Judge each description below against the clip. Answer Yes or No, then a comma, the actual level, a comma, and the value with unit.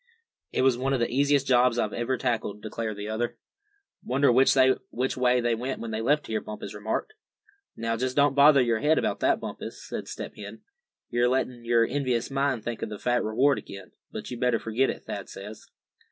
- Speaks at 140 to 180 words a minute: No, average, 200 wpm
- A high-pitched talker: No, low, 120 Hz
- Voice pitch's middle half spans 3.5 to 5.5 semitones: No, average, 2.8 semitones